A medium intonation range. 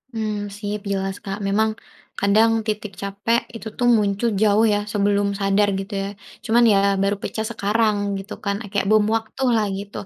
No: narrow, 1.6 semitones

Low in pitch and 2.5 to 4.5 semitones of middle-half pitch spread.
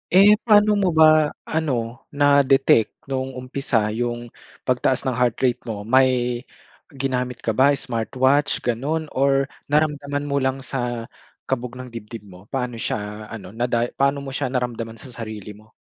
Yes: low, 125 Hz; average, 3.2 semitones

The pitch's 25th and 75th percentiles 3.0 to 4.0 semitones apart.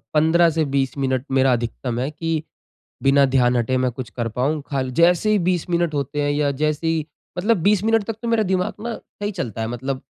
No: average, 5.0 semitones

